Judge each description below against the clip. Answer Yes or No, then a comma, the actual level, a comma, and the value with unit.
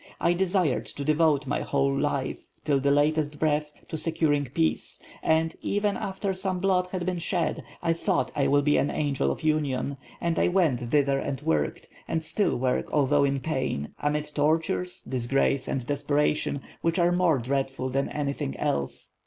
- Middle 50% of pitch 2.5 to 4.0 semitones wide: Yes, average, 3.3 semitones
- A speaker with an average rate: Yes, average, 170 wpm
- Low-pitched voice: No, medium, 150 Hz